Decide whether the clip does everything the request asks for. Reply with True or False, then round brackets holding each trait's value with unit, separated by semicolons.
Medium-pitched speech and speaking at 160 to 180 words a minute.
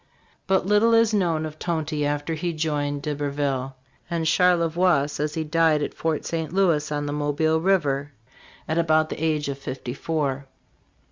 True (155 Hz; 165 wpm)